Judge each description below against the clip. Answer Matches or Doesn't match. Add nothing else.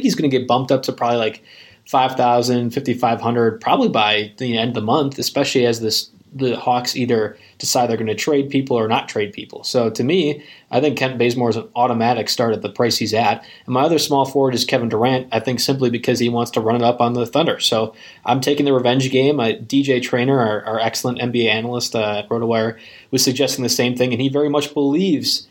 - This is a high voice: Doesn't match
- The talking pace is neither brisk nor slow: Doesn't match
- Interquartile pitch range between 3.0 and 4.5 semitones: Doesn't match